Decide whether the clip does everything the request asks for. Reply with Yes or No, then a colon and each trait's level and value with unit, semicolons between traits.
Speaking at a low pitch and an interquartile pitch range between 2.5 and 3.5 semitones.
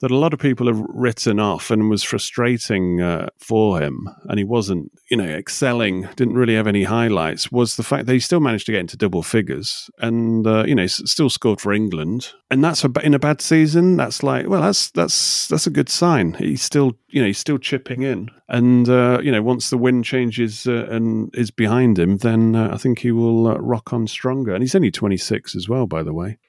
Yes: low, 120 Hz; average, 2.9 semitones